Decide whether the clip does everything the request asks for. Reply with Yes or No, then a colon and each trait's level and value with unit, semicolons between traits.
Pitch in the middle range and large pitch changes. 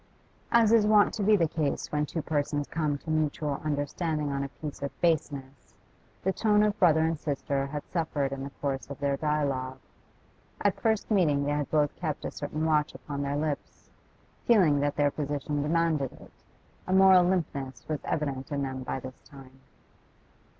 No: medium, 150 Hz; average, 2.9 semitones